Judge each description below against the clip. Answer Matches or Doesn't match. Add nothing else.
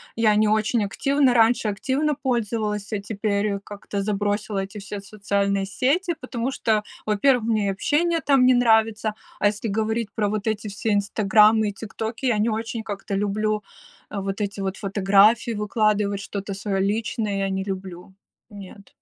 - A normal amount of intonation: Doesn't match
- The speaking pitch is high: Matches